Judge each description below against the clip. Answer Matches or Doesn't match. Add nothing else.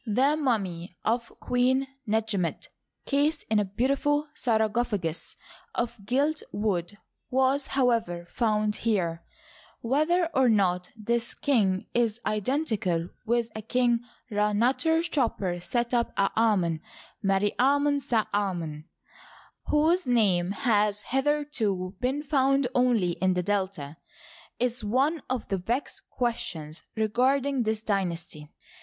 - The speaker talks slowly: Matches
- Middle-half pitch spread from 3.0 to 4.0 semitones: Doesn't match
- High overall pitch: Matches